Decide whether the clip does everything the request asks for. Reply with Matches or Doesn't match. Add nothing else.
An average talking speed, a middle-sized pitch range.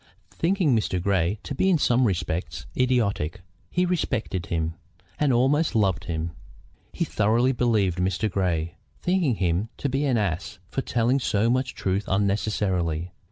Doesn't match